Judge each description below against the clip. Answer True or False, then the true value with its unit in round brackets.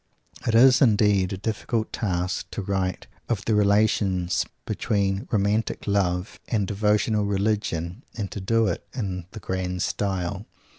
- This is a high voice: False (100 Hz)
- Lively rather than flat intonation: False (2.6 semitones)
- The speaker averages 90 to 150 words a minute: True (140 wpm)